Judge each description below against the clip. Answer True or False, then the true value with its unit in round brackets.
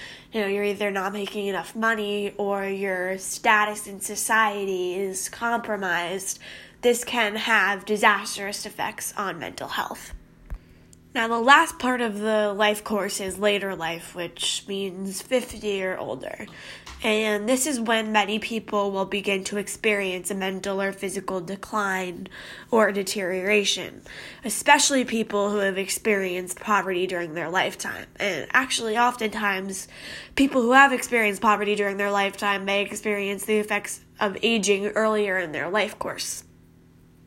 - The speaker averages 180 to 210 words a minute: False (140 wpm)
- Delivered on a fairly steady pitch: True (2.1 semitones)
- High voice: True (205 Hz)